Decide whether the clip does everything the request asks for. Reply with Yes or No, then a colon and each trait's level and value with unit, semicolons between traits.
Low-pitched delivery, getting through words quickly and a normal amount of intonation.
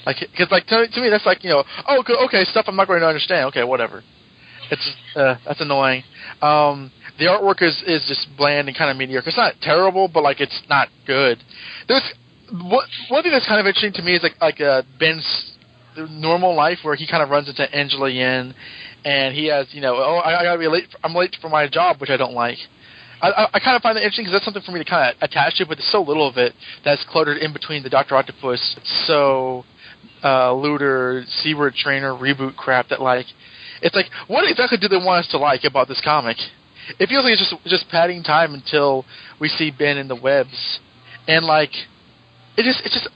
No: medium, 150 Hz; fast, 225 wpm; average, 4.9 semitones